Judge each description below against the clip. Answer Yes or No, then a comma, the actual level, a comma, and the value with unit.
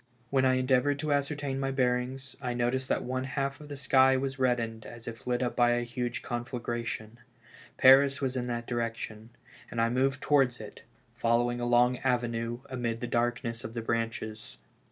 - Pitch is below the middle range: Yes, low, 125 Hz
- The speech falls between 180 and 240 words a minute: Yes, average, 185 wpm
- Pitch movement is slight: Yes, narrow, 2.0 semitones